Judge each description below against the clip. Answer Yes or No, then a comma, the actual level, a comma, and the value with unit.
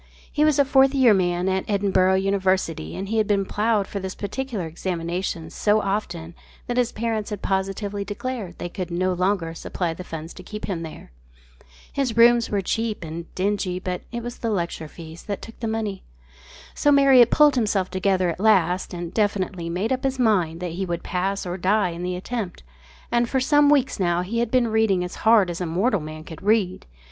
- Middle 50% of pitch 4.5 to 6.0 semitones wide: No, average, 4.1 semitones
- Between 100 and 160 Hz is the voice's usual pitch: No, high, 195 Hz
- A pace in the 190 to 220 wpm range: Yes, average, 200 wpm